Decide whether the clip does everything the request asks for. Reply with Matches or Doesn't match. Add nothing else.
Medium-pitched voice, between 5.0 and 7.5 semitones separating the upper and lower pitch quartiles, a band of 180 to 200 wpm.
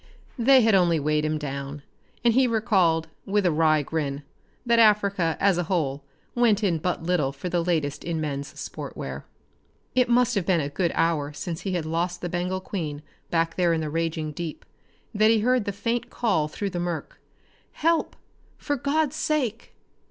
Matches